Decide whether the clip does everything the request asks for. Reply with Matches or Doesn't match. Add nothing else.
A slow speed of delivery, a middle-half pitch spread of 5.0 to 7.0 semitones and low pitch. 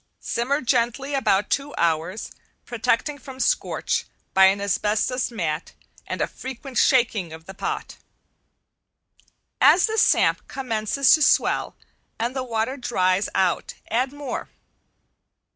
Doesn't match